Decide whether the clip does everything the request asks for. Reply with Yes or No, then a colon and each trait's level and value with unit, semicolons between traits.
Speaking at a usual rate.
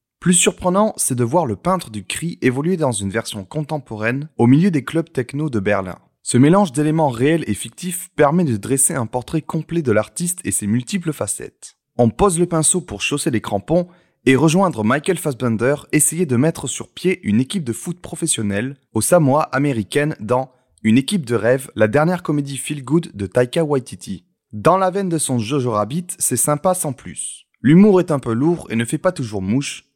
Yes: average, 200 wpm